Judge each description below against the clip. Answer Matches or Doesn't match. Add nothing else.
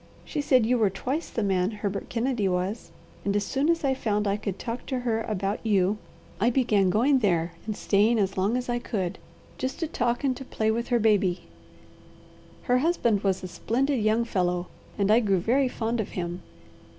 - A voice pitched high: Matches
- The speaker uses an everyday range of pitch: Matches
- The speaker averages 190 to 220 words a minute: Matches